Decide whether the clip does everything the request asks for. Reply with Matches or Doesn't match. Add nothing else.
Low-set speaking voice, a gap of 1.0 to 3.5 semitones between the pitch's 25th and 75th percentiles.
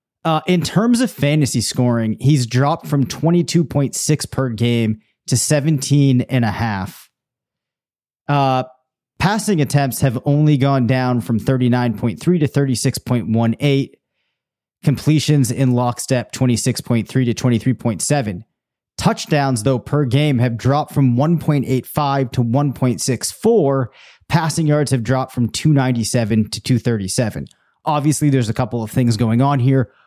Matches